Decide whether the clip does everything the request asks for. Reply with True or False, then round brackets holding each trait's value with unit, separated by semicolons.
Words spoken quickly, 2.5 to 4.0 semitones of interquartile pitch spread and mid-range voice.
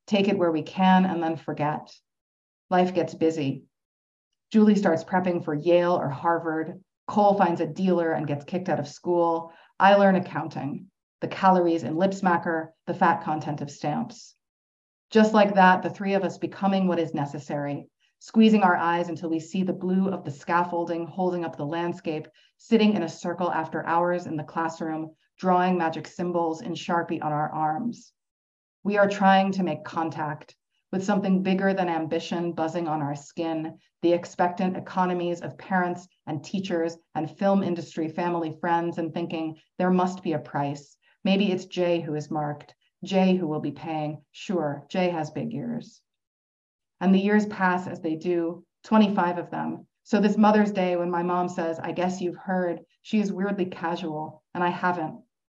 False (175 wpm; 2.8 semitones; 170 Hz)